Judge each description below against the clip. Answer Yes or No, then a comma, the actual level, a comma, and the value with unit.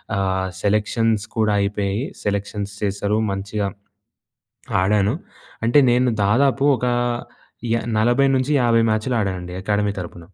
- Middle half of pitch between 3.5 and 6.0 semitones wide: No, average, 2.9 semitones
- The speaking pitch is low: Yes, low, 105 Hz